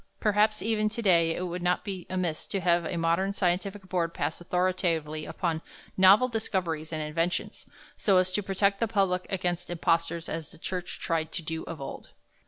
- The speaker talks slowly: No, average, 185 wpm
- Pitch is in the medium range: Yes, medium, 180 Hz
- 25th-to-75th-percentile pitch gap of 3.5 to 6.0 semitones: No, average, 2.8 semitones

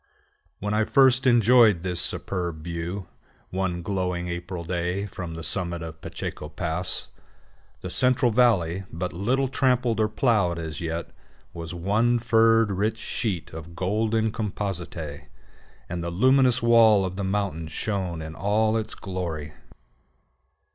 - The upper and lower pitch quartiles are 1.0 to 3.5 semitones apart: No, average, 4.6 semitones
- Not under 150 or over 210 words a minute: No, average, 140 wpm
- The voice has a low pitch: Yes, very low, 95 Hz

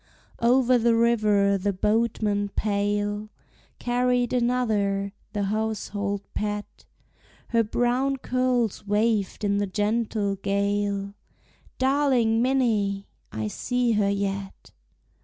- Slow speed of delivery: Yes, slow, 100 wpm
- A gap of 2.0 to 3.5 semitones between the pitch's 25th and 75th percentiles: Yes, average, 2.9 semitones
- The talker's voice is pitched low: No, high, 210 Hz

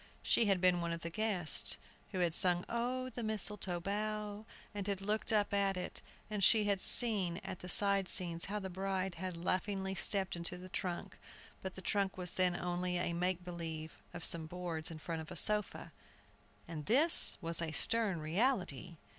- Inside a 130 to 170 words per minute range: No, average, 190 wpm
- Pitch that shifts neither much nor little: Yes, average, 3.0 semitones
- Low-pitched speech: No, medium, 185 Hz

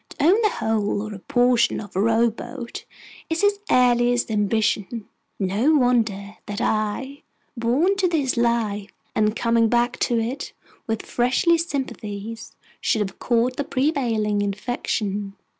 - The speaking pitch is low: No, high, 230 Hz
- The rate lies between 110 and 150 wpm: Yes, average, 140 wpm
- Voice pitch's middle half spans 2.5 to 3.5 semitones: Yes, average, 3.2 semitones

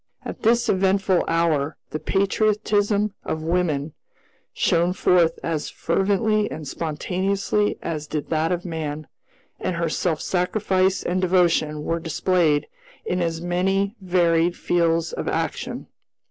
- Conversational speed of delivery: No, slow, 125 wpm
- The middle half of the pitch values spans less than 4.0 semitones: Yes, average, 3.0 semitones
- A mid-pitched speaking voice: Yes, medium, 175 Hz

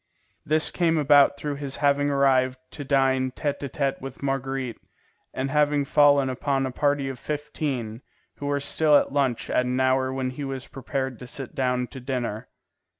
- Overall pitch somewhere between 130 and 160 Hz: Yes, low, 135 Hz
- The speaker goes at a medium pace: Yes, average, 185 wpm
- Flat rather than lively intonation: Yes, narrow, 1.7 semitones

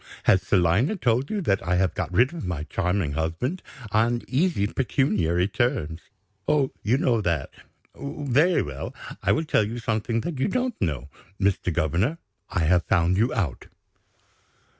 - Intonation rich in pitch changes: Yes, wide, 7.3 semitones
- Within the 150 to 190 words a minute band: Yes, average, 160 wpm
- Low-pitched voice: Yes, low, 105 Hz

